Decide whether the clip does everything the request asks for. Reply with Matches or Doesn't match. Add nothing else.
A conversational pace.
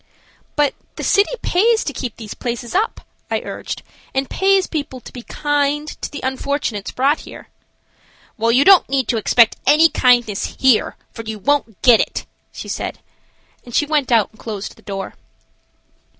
Matches